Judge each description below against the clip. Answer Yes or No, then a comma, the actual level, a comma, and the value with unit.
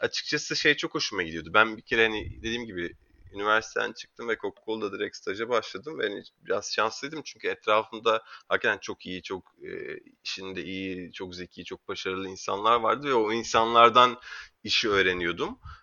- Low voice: Yes, low, 110 Hz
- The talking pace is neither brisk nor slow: No, fast, 155 wpm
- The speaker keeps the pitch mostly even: No, average, 5.0 semitones